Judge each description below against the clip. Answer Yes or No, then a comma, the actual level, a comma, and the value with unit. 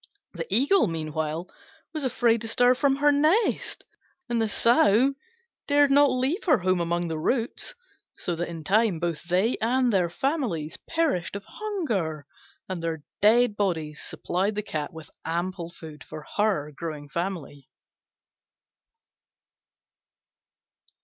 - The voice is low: No, high, 195 Hz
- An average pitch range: No, wide, 7.4 semitones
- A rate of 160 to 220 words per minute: No, slow, 135 wpm